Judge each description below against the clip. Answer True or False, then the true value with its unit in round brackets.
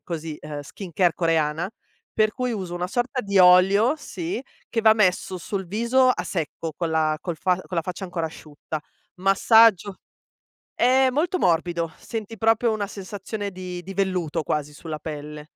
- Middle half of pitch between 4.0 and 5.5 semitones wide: True (4.8 semitones)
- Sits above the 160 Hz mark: True (185 Hz)